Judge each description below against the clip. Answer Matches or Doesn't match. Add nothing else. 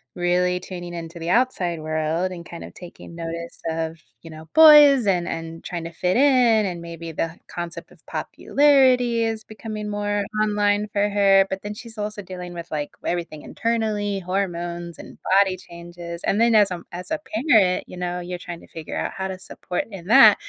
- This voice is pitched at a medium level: Matches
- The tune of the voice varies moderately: Matches